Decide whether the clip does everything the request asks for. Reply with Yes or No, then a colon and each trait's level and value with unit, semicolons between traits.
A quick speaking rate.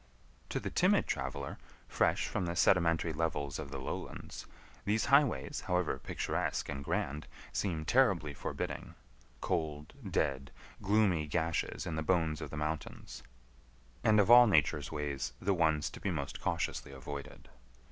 No: average, 140 wpm